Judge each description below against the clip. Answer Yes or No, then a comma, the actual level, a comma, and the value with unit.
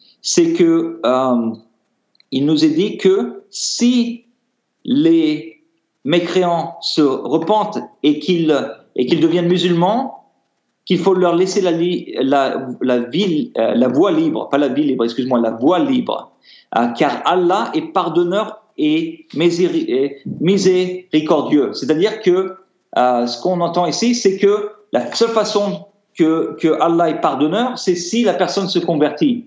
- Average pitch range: No, wide, 5.7 semitones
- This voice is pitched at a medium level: Yes, medium, 180 Hz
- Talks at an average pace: No, slow, 140 wpm